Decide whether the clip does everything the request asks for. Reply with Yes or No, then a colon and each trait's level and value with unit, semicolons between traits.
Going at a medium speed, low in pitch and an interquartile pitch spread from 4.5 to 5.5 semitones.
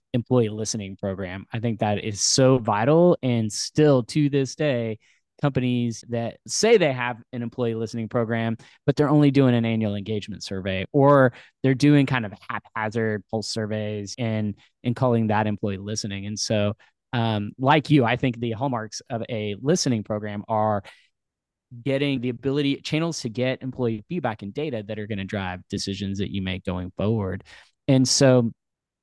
No: average, 170 wpm; low, 115 Hz; average, 3.7 semitones